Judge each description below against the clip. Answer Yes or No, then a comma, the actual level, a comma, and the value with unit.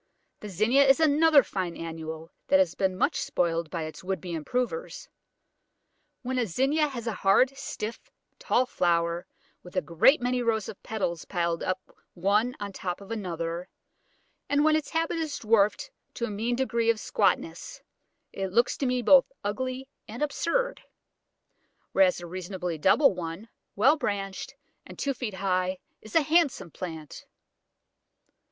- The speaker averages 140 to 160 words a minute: Yes, average, 155 wpm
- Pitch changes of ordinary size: No, wide, 6.4 semitones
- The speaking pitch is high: Yes, high, 210 Hz